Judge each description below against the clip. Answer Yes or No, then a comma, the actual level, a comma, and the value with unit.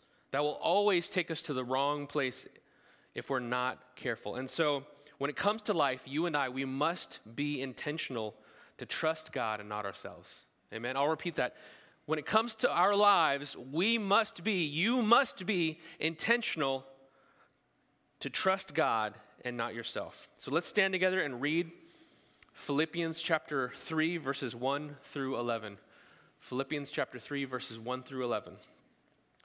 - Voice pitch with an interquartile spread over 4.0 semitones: Yes, average, 4.9 semitones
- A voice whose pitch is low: No, medium, 145 Hz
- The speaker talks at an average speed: Yes, average, 155 wpm